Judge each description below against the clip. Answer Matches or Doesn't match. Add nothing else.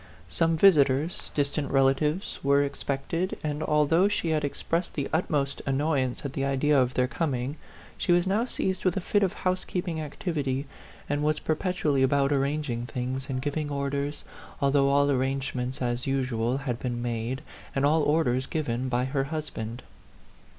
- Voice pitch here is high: Doesn't match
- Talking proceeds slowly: Doesn't match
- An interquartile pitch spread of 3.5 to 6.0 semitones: Doesn't match